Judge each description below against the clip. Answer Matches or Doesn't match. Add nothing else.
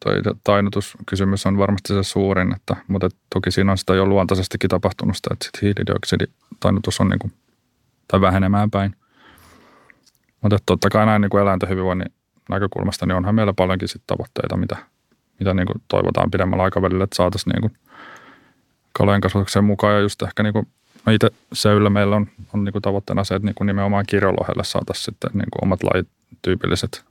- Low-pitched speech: Matches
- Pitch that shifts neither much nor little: Doesn't match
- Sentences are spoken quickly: Matches